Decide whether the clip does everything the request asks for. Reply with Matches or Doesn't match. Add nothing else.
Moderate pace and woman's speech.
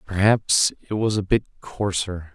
Doesn't match